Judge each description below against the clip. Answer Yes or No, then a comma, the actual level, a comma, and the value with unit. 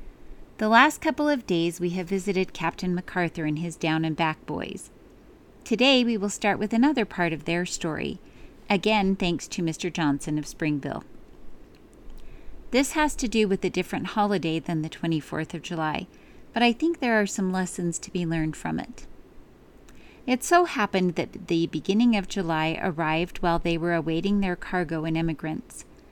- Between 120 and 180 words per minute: Yes, average, 170 wpm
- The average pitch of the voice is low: No, medium, 180 Hz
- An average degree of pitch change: Yes, average, 4.1 semitones